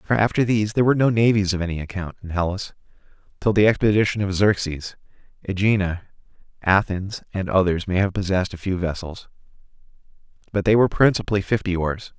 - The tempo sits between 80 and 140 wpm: No, average, 165 wpm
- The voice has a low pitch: Yes, very low, 95 Hz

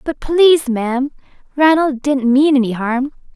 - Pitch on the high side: Yes, very high, 270 Hz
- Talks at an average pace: Yes, average, 145 wpm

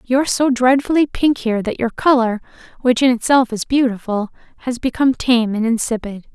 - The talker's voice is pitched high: Yes, high, 245 Hz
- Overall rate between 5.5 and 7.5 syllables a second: Yes, 5.6 syllables/s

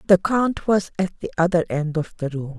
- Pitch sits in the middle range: Yes, medium, 175 Hz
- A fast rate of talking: Yes, fast, 230 wpm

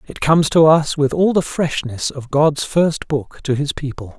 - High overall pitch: No, medium, 150 Hz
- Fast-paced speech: Yes, fast, 215 wpm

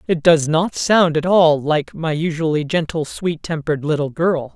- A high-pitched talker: No, medium, 160 Hz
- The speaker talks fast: No, average, 185 wpm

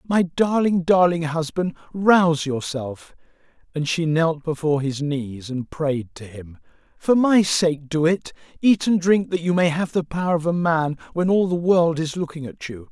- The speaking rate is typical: Yes, average, 190 wpm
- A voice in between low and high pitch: Yes, medium, 160 Hz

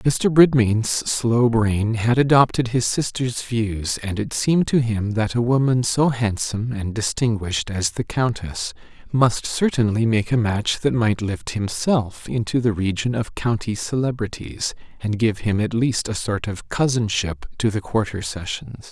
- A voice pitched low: Yes, low, 110 Hz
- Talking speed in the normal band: Yes, average, 165 wpm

